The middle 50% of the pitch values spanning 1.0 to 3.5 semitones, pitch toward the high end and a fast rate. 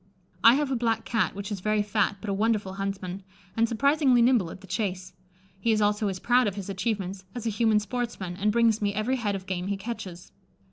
Yes: average, 3.0 semitones; high, 210 Hz; fast, 225 wpm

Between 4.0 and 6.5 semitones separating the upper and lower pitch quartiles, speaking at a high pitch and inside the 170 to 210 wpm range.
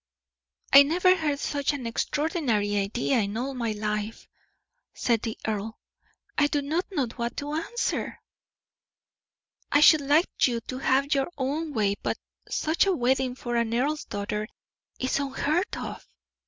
No: average, 4.6 semitones; very high, 265 Hz; average, 150 wpm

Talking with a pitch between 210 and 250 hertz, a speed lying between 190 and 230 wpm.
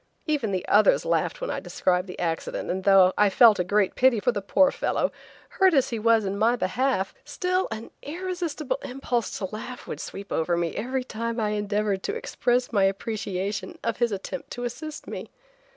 Yes: high, 225 Hz; average, 195 wpm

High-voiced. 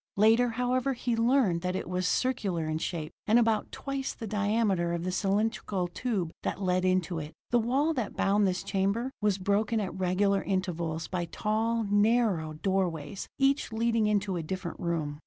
Yes: high, 200 Hz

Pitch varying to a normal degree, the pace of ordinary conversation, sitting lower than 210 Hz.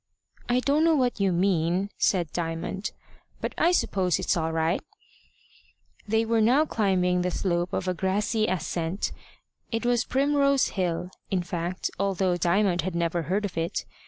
Yes: average, 4.3 semitones; average, 160 wpm; medium, 185 Hz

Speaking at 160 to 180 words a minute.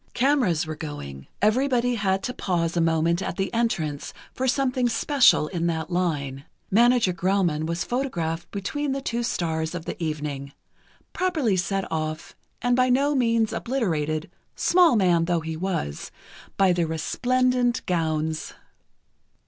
No: average, 140 wpm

